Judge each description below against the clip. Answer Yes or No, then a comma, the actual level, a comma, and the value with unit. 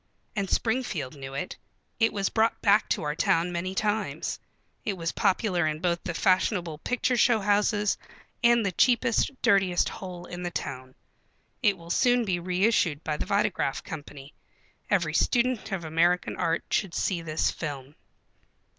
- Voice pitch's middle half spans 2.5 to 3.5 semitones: No, average, 4.4 semitones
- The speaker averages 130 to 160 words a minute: Yes, average, 155 wpm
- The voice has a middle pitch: Yes, medium, 180 Hz